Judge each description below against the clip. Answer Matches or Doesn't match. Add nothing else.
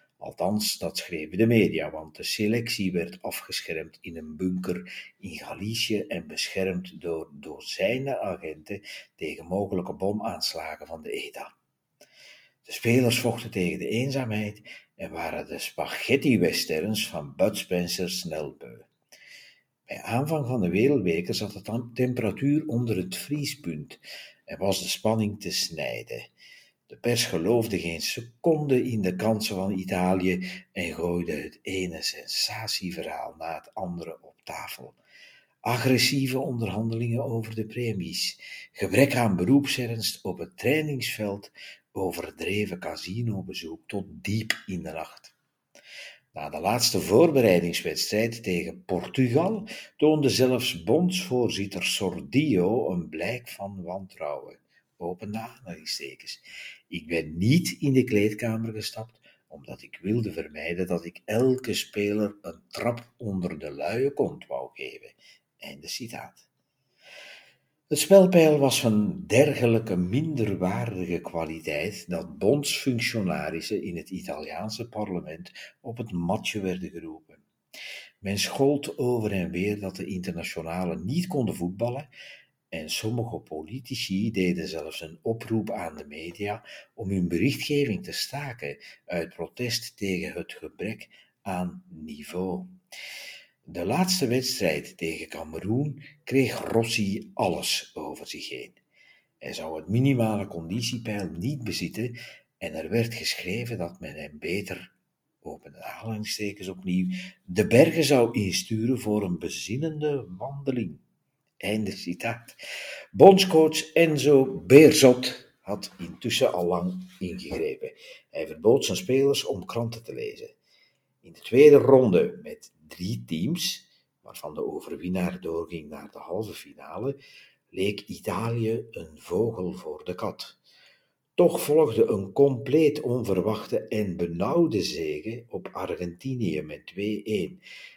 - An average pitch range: Doesn't match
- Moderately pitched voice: Doesn't match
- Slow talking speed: Matches